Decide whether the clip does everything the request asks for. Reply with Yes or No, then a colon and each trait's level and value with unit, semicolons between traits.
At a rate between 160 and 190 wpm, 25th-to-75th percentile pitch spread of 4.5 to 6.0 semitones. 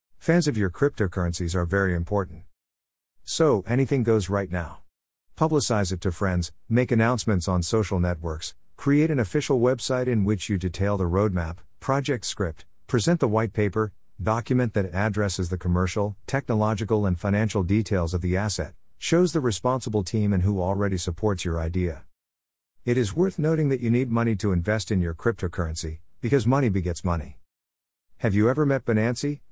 Yes: average, 165 wpm; average, 4.9 semitones